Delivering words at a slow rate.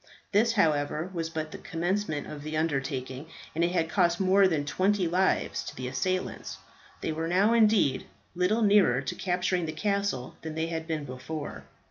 No: average, 175 wpm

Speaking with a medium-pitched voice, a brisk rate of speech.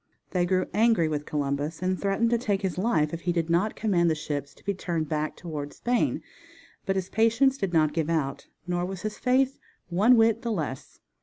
Yes: medium, 180 Hz; fast, 210 wpm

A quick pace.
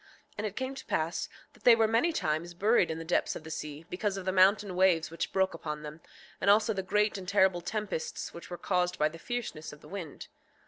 Yes: fast, 240 wpm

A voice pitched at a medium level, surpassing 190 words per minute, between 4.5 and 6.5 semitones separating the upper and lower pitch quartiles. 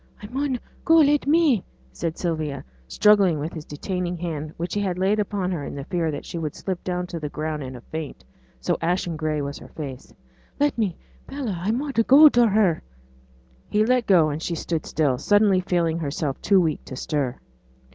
Yes: medium, 175 Hz; average, 200 wpm; average, 5.1 semitones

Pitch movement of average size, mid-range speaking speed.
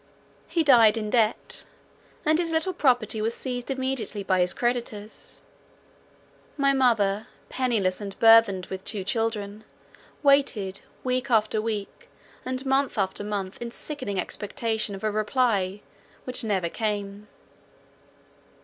No: average, 3.9 semitones; slow, 125 wpm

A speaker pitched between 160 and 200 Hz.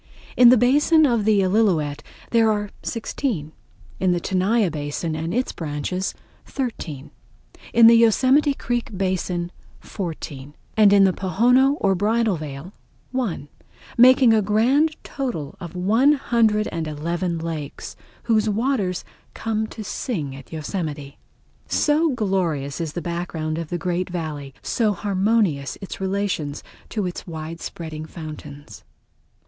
Yes: high, 190 Hz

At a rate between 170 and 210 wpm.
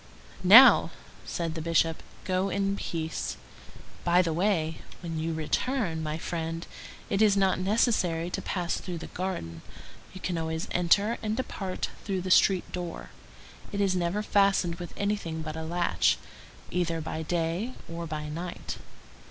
No: average, 150 wpm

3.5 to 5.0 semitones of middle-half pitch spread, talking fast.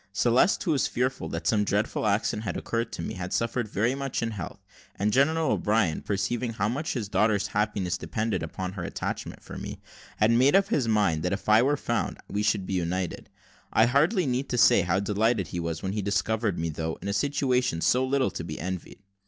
Yes: average, 4.5 semitones; fast, 210 wpm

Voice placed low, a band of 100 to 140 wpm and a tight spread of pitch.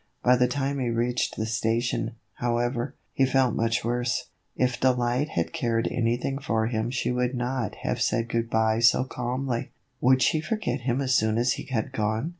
No: low, 120 Hz; average, 185 wpm; narrow, 1.9 semitones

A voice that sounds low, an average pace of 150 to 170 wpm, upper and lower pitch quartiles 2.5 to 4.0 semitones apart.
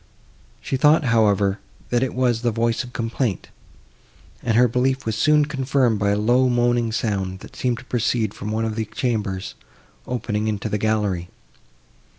Yes: low, 115 Hz; average, 165 wpm; average, 2.9 semitones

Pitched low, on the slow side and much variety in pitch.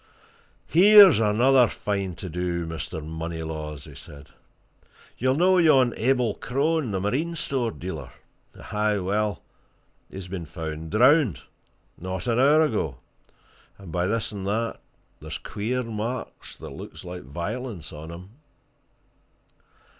Yes: low, 105 Hz; slow, 125 wpm; wide, 6.9 semitones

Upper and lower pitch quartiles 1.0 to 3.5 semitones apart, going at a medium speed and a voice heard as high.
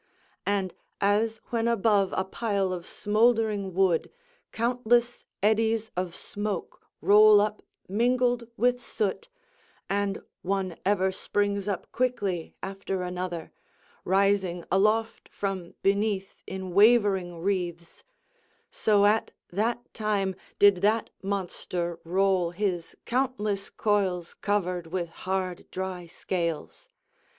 No: average, 2.7 semitones; slow, 105 wpm; high, 200 Hz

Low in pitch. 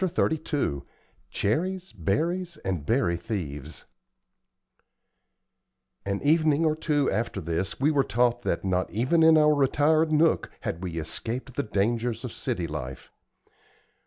Yes: low, 120 Hz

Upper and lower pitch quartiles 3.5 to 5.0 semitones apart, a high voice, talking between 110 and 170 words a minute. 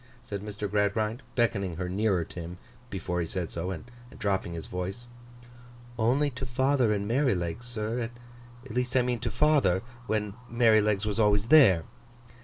No: average, 4.1 semitones; low, 105 Hz; average, 160 wpm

